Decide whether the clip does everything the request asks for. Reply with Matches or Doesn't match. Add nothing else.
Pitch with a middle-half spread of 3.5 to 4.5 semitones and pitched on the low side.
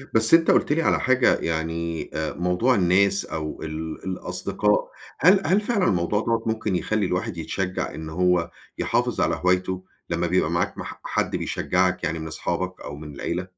Matches